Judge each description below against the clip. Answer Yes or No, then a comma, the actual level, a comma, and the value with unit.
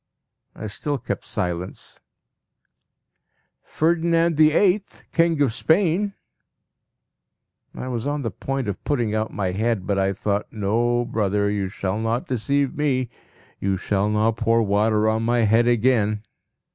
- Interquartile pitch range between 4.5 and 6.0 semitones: Yes, average, 5.2 semitones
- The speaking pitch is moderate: No, low, 115 Hz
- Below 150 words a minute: Yes, average, 140 wpm